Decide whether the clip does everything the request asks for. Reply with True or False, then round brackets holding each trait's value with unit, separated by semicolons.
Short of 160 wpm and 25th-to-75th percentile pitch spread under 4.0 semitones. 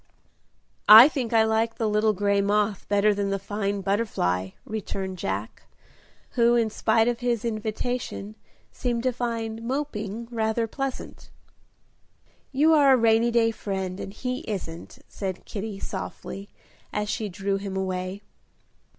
True (140 wpm; 2.9 semitones)